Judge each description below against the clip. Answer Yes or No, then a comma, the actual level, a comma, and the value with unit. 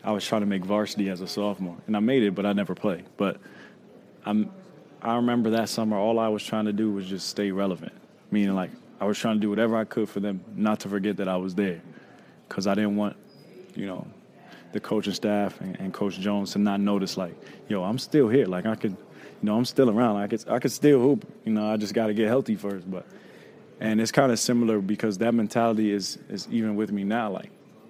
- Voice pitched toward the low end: Yes, low, 105 Hz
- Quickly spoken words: Yes, fast, 240 wpm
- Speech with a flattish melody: Yes, narrow, 2.0 semitones